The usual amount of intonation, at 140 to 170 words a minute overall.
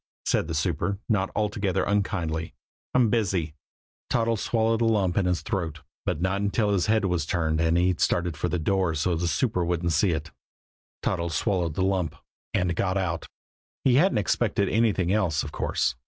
No: average, 3.6 semitones; average, 185 wpm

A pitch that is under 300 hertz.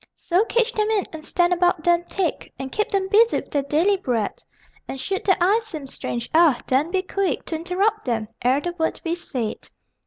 No: very high, 345 Hz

